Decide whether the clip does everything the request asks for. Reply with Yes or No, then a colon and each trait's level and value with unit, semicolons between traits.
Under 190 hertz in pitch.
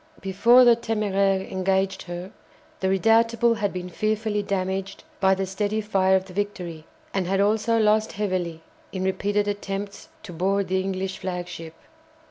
No: high, 195 Hz